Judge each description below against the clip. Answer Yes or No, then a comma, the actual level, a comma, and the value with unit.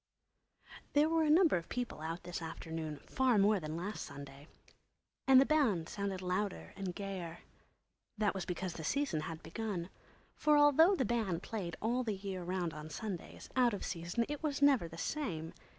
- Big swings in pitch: Yes, wide, 7.1 semitones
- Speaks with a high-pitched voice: Yes, high, 195 Hz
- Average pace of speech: Yes, average, 180 wpm